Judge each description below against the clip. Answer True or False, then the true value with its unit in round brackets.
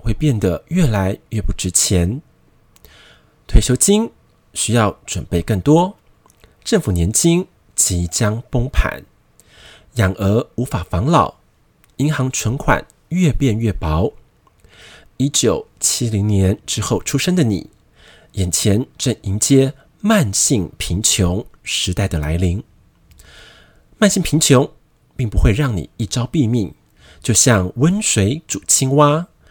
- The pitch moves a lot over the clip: True (6.8 semitones)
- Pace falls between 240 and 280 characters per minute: False (175 characters per minute)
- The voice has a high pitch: False (115 Hz)